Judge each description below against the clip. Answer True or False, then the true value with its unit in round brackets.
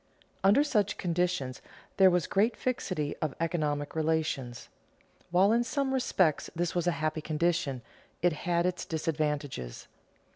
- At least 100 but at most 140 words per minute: True (135 wpm)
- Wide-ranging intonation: False (3.5 semitones)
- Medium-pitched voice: True (170 Hz)